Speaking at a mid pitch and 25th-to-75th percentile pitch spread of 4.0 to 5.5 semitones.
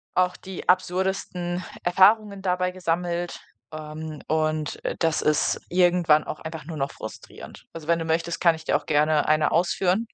No: medium, 170 Hz; average, 2.7 semitones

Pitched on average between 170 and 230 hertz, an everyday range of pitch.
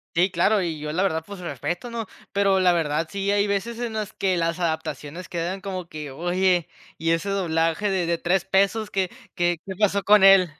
Yes: medium, 185 Hz; average, 3.0 semitones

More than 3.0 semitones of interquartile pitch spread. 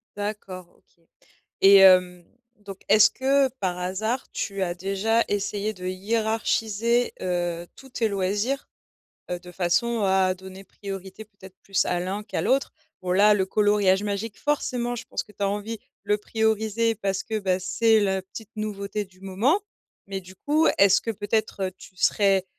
No: average, 2.7 semitones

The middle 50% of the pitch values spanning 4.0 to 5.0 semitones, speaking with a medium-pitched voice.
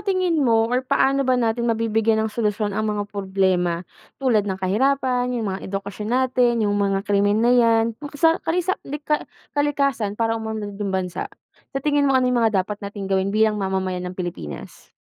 No: average, 4.4 semitones; high, 220 Hz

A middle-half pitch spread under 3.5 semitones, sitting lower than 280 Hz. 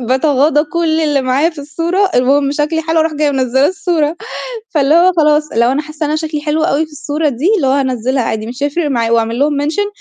No: average, 3.1 semitones; very high, 295 Hz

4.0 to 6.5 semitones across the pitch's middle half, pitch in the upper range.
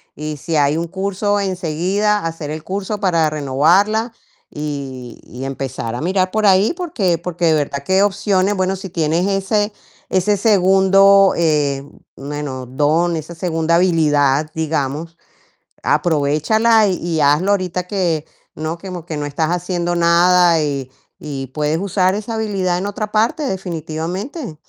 No: average, 4.3 semitones; medium, 175 Hz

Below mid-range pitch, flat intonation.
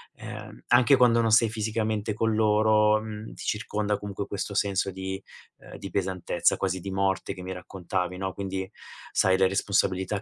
Yes: low, 100 Hz; narrow, 2.1 semitones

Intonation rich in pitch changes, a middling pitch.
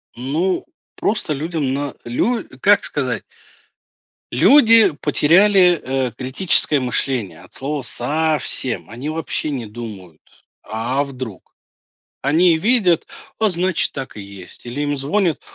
Yes: wide, 6.0 semitones; medium, 145 Hz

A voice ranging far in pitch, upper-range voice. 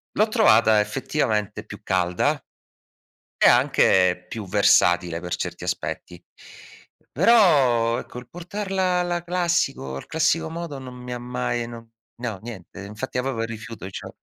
No: wide, 7.5 semitones; low, 120 Hz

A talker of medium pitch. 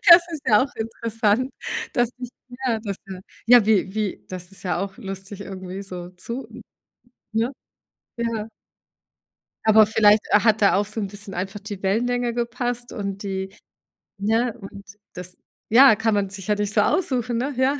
No: high, 210 Hz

